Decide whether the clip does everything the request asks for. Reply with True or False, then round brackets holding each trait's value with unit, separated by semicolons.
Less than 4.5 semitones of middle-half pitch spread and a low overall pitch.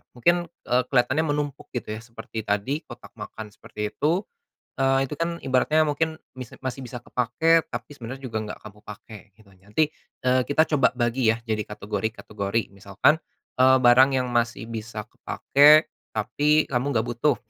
False (4.8 semitones; 125 Hz)